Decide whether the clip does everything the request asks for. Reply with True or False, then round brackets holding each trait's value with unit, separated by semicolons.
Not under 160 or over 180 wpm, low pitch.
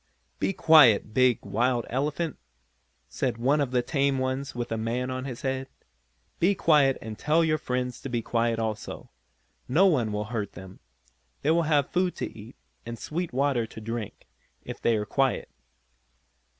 True (170 wpm; 130 Hz)